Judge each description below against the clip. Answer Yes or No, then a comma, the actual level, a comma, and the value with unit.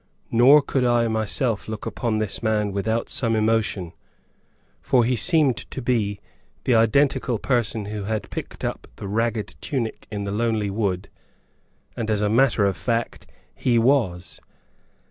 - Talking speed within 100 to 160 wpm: Yes, average, 150 wpm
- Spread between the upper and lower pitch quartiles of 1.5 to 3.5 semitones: Yes, average, 2.7 semitones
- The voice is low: Yes, low, 110 Hz